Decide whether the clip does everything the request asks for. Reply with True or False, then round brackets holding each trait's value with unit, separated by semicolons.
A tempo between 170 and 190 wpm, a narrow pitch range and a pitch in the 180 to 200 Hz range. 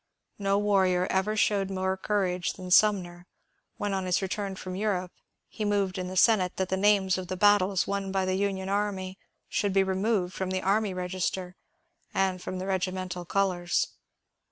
True (175 wpm; 1.4 semitones; 190 Hz)